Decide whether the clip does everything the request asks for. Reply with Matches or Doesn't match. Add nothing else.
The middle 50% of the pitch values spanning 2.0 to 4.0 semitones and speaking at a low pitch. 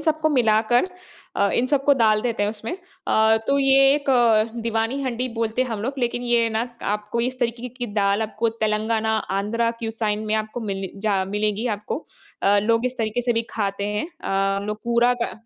Doesn't match